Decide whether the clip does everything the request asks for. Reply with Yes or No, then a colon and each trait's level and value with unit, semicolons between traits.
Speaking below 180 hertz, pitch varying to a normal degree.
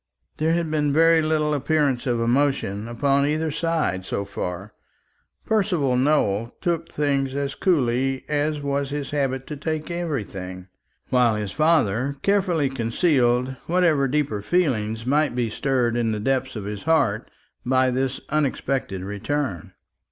Yes: low, 135 Hz; average, 4.6 semitones